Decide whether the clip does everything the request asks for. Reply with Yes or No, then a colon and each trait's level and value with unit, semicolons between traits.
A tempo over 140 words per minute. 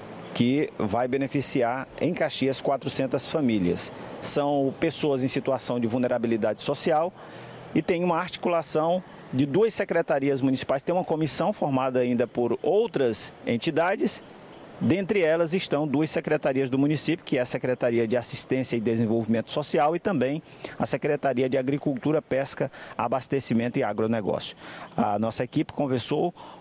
No: average, 135 wpm